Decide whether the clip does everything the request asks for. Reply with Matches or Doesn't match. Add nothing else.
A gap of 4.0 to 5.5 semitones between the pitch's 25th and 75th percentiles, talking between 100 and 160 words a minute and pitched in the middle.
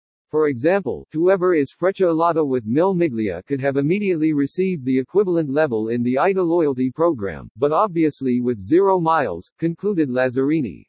Matches